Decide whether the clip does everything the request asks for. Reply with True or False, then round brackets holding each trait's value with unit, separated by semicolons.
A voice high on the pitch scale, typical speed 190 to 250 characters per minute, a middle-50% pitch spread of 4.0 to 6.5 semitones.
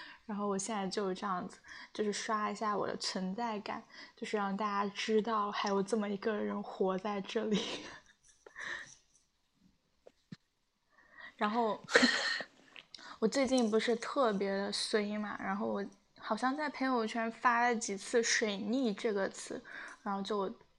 False (215 Hz; 205 characters per minute; 2.5 semitones)